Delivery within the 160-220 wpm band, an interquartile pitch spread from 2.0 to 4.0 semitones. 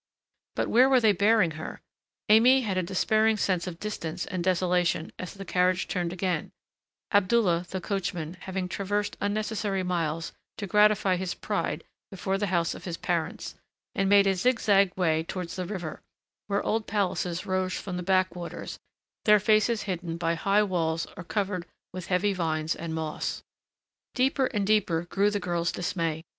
Yes: average, 165 wpm; average, 3.0 semitones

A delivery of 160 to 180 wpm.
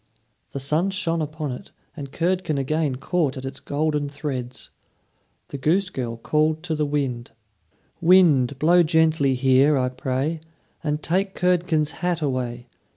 No: average, 145 wpm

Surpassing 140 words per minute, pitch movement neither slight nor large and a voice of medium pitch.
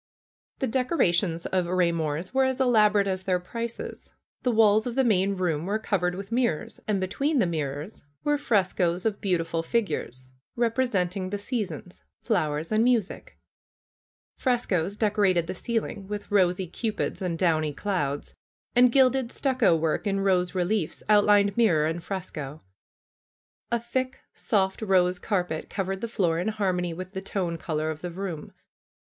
No: average, 150 wpm; average, 4.2 semitones; high, 195 Hz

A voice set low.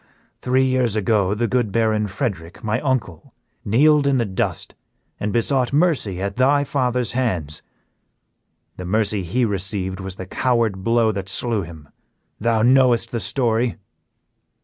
Yes: low, 115 Hz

